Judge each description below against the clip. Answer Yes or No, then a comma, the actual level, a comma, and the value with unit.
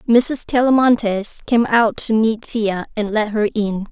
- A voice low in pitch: No, high, 220 Hz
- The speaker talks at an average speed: Yes, average, 170 wpm